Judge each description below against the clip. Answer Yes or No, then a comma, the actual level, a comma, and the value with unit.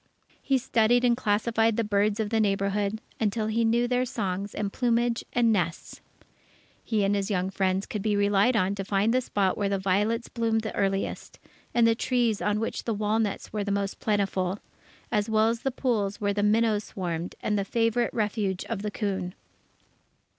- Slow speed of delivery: No, average, 185 wpm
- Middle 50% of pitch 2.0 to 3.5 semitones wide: Yes, narrow, 2.4 semitones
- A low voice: No, high, 210 Hz